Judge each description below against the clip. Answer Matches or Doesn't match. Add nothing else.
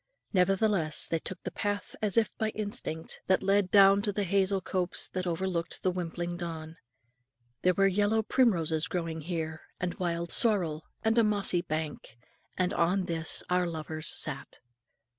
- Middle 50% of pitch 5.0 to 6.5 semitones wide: Doesn't match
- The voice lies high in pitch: Doesn't match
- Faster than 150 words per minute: Matches